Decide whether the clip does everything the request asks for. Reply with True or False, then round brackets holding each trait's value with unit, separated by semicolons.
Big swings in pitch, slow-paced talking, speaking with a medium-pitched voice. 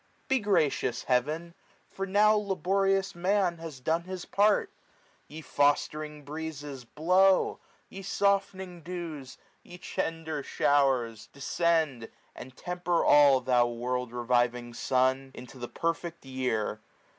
True (5.8 semitones; 120 wpm; 155 Hz)